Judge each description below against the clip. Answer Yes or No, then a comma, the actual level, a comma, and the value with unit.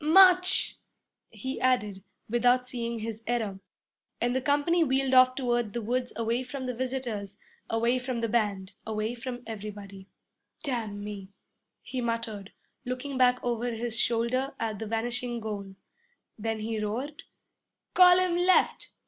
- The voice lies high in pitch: Yes, high, 240 Hz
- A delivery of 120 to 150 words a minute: Yes, average, 140 wpm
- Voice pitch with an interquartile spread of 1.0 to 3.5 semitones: Yes, average, 2.8 semitones